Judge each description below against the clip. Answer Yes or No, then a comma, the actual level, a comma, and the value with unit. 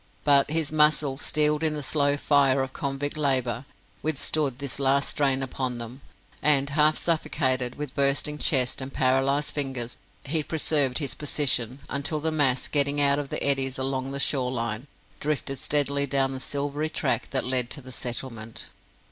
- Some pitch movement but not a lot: No, narrow, 2.0 semitones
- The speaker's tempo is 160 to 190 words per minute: Yes, average, 165 wpm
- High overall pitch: No, medium, 140 Hz